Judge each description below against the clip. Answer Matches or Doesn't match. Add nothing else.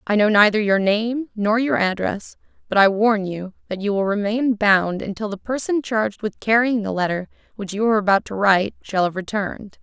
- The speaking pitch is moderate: Doesn't match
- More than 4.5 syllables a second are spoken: Matches